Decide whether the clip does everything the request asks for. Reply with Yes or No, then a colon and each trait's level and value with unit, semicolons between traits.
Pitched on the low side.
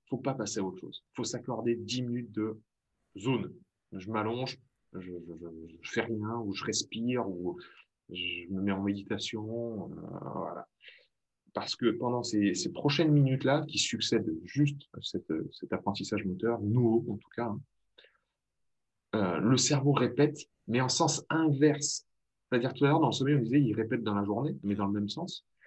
Yes: low, 115 Hz